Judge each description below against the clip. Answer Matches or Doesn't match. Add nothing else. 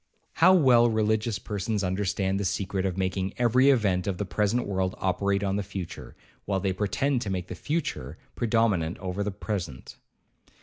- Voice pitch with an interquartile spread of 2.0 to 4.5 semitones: Matches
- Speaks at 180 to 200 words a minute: Doesn't match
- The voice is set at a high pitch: Doesn't match